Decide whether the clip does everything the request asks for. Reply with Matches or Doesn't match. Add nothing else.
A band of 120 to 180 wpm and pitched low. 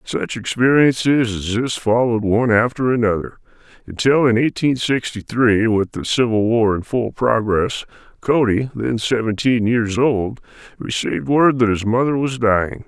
Matches